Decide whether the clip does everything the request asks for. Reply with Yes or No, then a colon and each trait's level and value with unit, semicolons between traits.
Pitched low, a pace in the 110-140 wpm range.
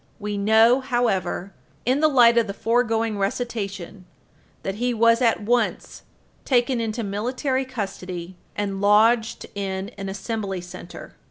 No: high, 220 Hz; slow, 135 wpm